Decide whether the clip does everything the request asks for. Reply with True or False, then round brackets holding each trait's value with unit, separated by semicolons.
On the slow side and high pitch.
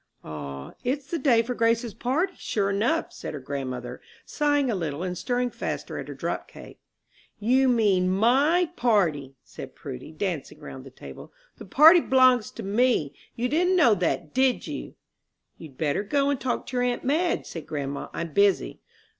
False (175 wpm; 230 Hz)